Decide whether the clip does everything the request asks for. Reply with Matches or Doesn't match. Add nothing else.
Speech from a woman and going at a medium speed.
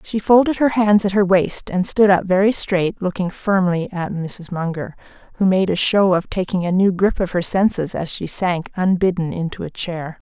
Doesn't match